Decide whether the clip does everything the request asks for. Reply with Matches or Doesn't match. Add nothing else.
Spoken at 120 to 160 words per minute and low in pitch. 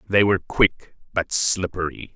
Matches